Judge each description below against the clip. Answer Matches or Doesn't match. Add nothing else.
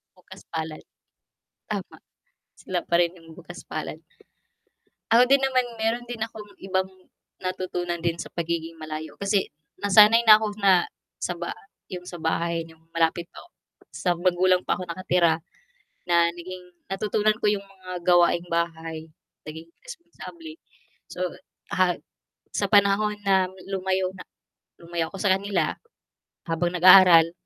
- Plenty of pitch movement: Doesn't match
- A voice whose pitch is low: Doesn't match